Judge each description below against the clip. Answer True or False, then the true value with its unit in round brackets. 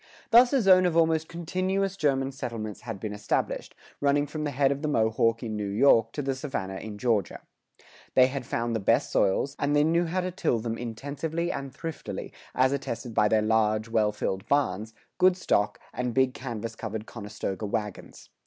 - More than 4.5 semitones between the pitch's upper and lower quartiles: True (5.6 semitones)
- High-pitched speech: False (125 Hz)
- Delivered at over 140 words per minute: True (190 wpm)